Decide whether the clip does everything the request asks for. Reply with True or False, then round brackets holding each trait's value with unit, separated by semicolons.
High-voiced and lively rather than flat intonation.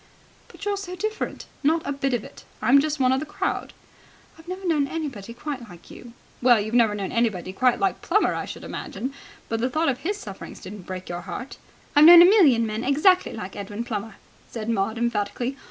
True (245 Hz; 6.3 semitones)